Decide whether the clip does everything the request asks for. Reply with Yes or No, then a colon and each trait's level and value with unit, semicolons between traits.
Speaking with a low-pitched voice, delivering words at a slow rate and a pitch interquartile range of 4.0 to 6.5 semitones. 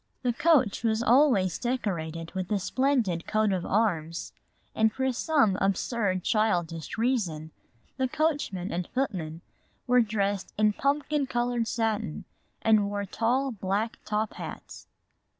No: high, 215 Hz; slow, 130 wpm; average, 4.8 semitones